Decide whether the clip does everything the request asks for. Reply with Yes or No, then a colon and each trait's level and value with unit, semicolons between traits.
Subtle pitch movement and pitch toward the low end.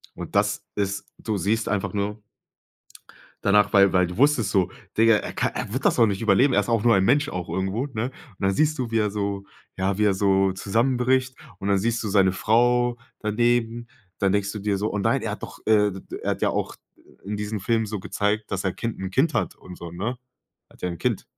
No: average, 3.2 semitones; low, 105 Hz